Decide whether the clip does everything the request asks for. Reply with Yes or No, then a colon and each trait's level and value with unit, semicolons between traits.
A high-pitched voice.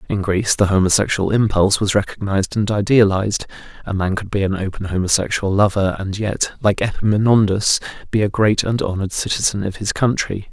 No: low, 100 Hz